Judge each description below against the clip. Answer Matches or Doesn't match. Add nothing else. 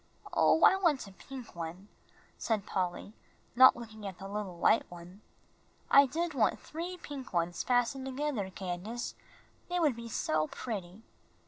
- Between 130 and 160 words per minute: Matches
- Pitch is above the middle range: Matches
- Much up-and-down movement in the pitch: Matches